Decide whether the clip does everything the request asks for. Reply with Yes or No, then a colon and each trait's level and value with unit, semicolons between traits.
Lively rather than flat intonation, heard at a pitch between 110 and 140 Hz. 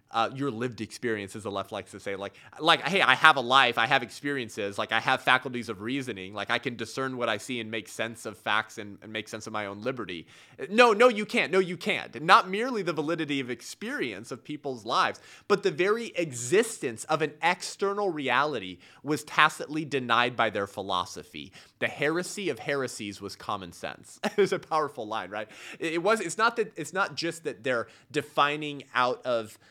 Yes: wide, 6.2 semitones; low, 135 Hz